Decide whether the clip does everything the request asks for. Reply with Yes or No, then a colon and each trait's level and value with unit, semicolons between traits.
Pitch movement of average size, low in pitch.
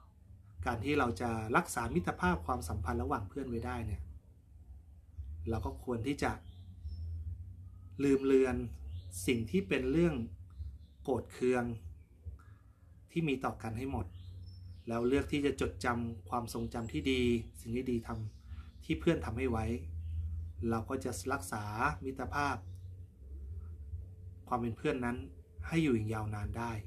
No: wide, 6.0 semitones; low, 100 Hz